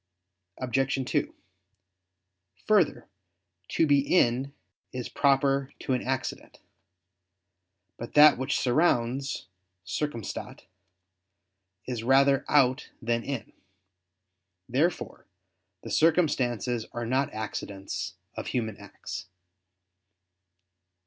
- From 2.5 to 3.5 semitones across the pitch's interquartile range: Yes, average, 2.9 semitones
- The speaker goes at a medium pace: No, slow, 85 wpm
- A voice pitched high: No, low, 130 Hz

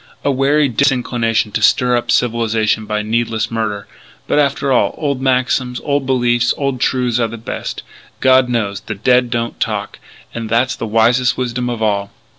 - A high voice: No, low, 120 Hz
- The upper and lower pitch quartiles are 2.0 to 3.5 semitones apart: Yes, narrow, 2.4 semitones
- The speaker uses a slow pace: No, average, 170 wpm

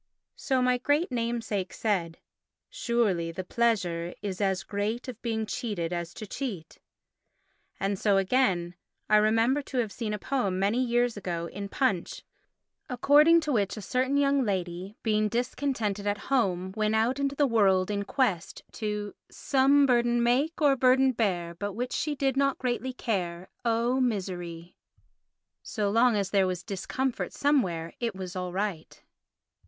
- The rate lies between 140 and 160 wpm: Yes, average, 155 wpm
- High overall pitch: Yes, high, 215 Hz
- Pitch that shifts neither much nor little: Yes, average, 5.0 semitones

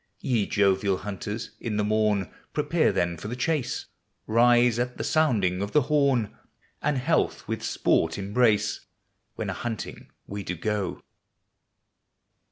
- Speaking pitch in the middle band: No, low, 110 Hz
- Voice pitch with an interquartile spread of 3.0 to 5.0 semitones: Yes, average, 3.7 semitones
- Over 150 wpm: No, average, 140 wpm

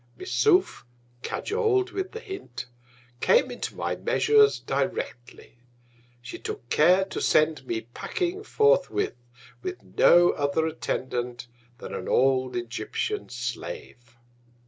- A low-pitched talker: No, medium, 175 Hz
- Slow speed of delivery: Yes, slow, 110 wpm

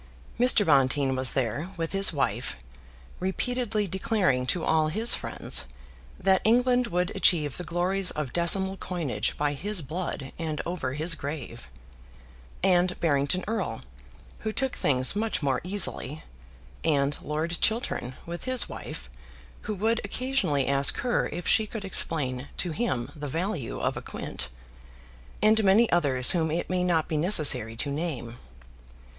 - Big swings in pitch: Yes, wide, 5.8 semitones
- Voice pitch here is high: No, medium, 170 Hz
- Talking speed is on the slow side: No, average, 145 wpm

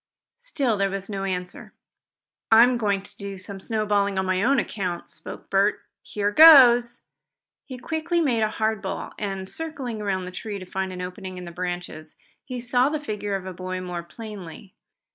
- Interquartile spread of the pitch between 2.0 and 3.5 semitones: No, average, 4.2 semitones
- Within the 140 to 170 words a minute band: No, average, 180 wpm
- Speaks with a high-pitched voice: Yes, high, 200 Hz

